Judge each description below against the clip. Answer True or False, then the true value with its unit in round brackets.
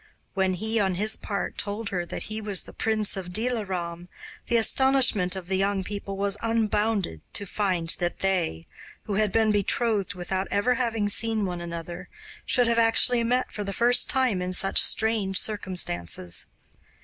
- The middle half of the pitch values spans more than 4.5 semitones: False (3.4 semitones)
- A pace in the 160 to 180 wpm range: True (170 wpm)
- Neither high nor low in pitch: False (200 Hz)